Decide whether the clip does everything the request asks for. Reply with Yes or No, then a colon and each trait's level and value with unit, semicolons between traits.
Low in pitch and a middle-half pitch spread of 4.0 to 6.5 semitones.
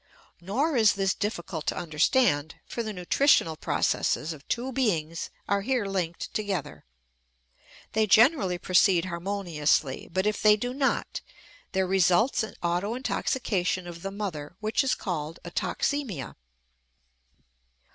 No: high, 195 Hz; average, 4.3 semitones